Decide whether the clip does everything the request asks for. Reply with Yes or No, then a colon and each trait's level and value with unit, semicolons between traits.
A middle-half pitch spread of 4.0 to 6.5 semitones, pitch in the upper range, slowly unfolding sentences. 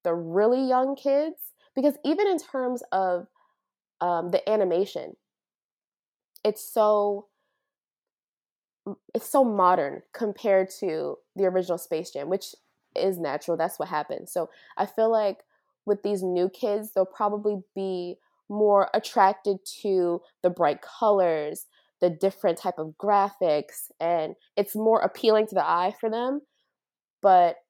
Yes: average, 4.6 semitones; high, 200 Hz; slow, 130 wpm